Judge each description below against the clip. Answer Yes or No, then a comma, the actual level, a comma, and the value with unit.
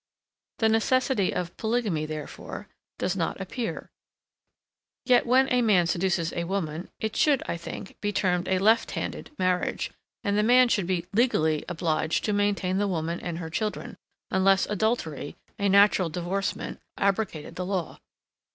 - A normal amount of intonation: Yes, average, 4.0 semitones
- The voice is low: No, high, 190 Hz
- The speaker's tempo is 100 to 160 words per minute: Yes, average, 150 wpm